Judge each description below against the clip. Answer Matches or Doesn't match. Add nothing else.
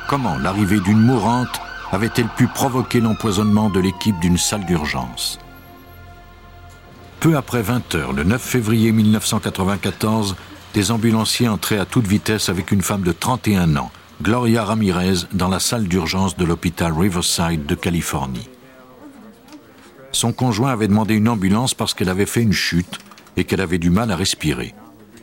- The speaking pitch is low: Matches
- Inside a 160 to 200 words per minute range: Doesn't match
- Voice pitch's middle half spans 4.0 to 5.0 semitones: Matches